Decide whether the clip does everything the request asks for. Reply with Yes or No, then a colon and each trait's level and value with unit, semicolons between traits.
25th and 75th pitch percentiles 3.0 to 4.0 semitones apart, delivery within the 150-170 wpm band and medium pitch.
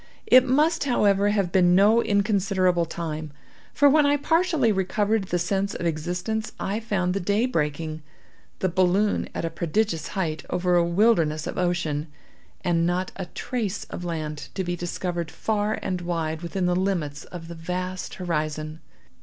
Yes: average, 3.5 semitones; average, 160 wpm; medium, 180 Hz